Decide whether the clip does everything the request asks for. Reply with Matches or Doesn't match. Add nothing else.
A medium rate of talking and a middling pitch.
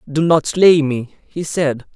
Matches